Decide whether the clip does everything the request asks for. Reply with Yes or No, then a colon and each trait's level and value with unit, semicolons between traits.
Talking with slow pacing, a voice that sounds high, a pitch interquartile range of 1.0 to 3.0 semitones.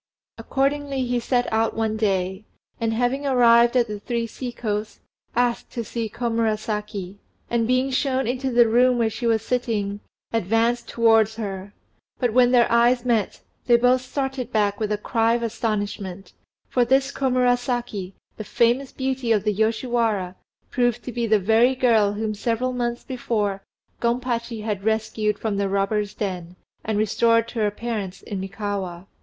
No: average, 160 wpm; high, 230 Hz; average, 2.7 semitones